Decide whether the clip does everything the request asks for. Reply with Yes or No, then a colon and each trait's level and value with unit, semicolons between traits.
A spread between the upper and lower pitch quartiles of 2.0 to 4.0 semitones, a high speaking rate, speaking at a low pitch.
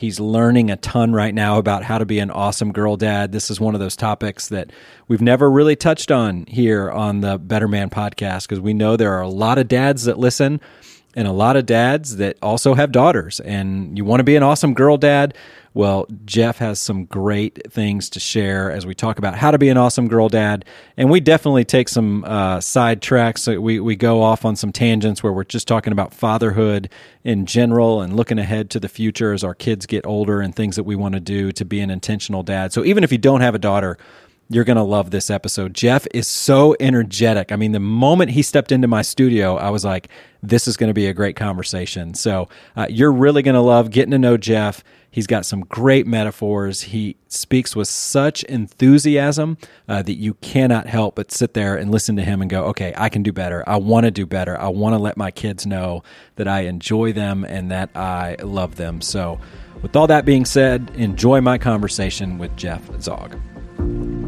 Yes: average, 3.3 semitones; fast, 225 wpm; low, 110 Hz